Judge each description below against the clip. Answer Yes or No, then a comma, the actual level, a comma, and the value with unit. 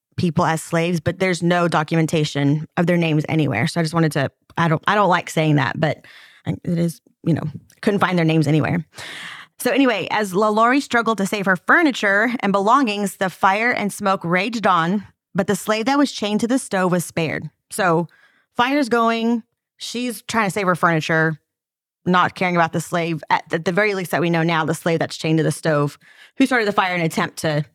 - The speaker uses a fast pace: Yes, fast, 215 wpm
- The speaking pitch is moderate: Yes, medium, 175 Hz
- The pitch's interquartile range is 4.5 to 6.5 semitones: Yes, average, 4.8 semitones